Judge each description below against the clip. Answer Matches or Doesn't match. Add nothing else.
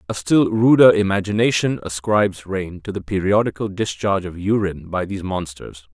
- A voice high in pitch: Doesn't match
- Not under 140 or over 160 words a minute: Matches